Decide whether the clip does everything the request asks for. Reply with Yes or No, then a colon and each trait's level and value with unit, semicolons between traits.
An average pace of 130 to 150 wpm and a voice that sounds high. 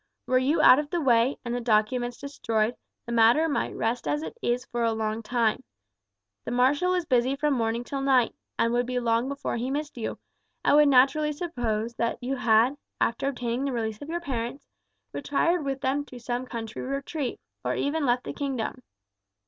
No: average, 195 wpm; very high, 250 Hz